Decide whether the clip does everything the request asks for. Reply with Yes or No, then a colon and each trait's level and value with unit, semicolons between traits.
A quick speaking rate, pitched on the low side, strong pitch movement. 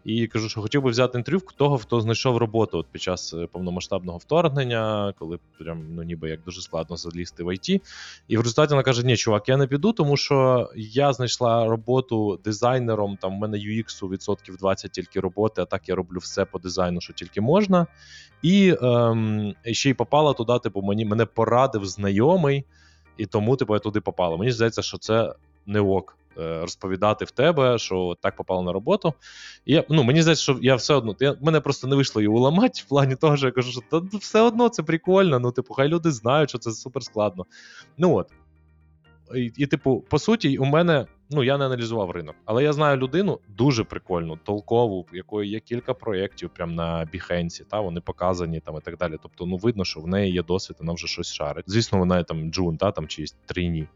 Yes: fast, 205 wpm; low, 110 Hz; wide, 6.7 semitones